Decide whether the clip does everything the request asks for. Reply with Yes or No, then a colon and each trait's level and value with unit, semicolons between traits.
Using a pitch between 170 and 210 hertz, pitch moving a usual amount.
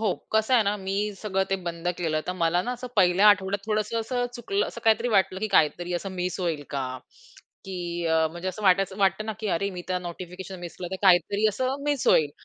Yes: high, 190 Hz; average, 3.4 semitones